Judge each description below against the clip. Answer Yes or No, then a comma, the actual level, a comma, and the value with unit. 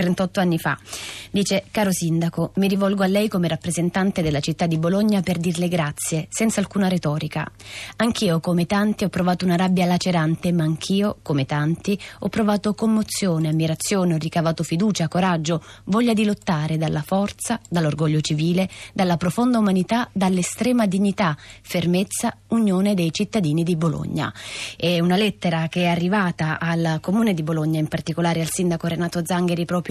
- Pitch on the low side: No, medium, 175 Hz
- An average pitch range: Yes, average, 3.3 semitones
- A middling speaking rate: Yes, average, 155 wpm